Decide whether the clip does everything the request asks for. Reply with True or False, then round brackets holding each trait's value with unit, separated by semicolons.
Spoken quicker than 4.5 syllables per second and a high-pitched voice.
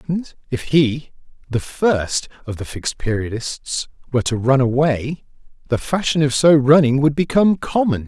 False (4.8 syllables/s; 140 Hz)